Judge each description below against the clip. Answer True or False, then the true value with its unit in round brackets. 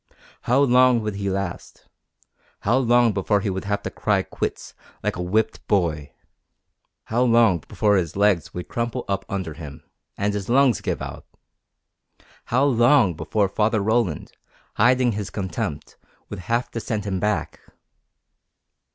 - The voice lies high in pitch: False (105 Hz)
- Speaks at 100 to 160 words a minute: True (150 wpm)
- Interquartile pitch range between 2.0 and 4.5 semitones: True (3.9 semitones)